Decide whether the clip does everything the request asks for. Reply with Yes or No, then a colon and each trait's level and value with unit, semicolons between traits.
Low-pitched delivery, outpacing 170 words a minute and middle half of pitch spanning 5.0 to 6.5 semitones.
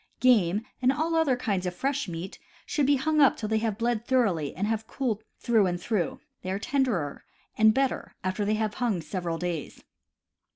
No: high, 220 Hz; average, 200 wpm; wide, 5.6 semitones